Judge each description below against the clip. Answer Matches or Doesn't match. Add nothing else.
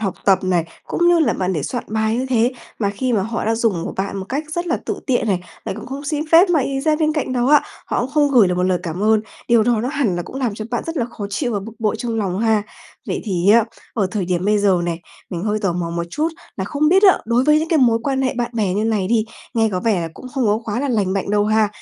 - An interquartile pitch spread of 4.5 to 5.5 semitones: Matches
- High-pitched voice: Matches